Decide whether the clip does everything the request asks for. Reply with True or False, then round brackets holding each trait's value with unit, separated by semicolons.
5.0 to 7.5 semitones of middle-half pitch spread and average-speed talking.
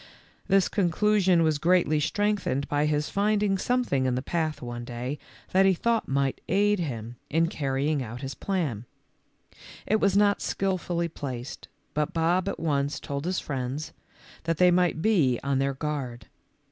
True (5.5 semitones; 160 wpm)